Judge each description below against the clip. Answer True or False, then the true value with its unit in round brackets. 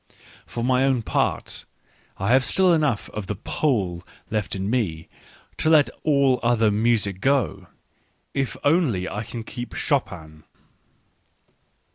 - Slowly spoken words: True (130 wpm)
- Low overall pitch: True (120 Hz)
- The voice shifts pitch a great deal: True (5.7 semitones)